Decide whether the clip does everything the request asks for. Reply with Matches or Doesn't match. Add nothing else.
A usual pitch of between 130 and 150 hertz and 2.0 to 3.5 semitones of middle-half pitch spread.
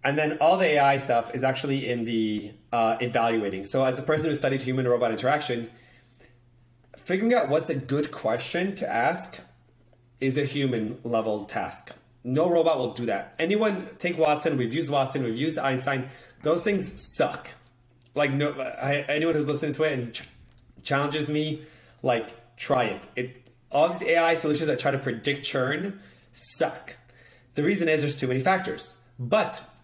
Doesn't match